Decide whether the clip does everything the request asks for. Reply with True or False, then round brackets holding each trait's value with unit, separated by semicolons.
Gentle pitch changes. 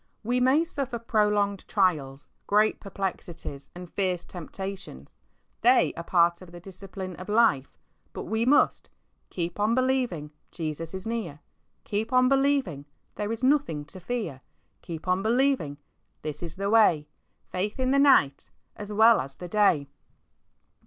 False (5.4 semitones)